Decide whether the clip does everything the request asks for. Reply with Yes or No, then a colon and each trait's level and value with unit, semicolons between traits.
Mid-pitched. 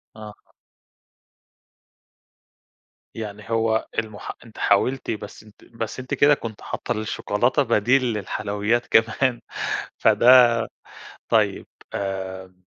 No: low, 110 Hz